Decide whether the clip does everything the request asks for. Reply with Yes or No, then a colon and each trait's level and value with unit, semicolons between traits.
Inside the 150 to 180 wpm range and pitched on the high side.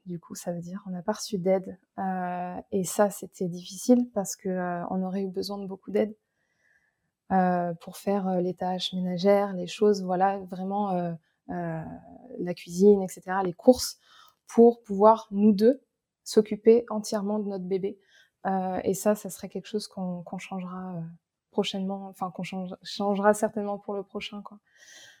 Yes: average, 170 wpm; high, 195 Hz